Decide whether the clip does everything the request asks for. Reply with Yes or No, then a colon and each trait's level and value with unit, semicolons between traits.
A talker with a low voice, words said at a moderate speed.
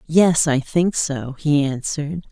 No: medium, 150 Hz; average, 155 wpm